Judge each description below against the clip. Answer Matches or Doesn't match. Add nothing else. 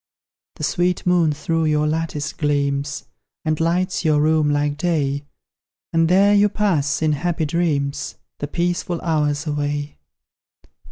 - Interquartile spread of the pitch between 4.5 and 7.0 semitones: Doesn't match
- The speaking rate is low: Matches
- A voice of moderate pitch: Matches